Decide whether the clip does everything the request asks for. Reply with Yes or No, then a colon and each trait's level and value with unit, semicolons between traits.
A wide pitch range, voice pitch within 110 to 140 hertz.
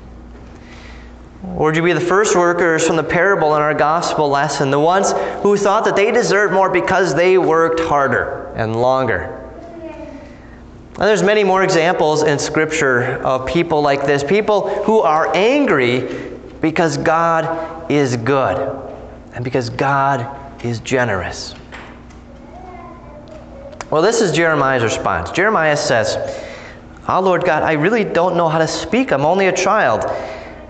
No: wide, 6.0 semitones; medium, 160 Hz